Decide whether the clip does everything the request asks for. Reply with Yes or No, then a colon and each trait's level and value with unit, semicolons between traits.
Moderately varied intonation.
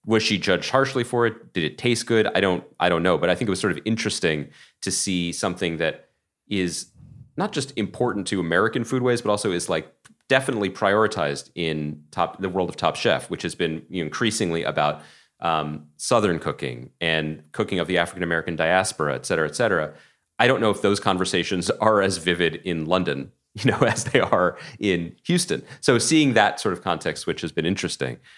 No: wide, 5.8 semitones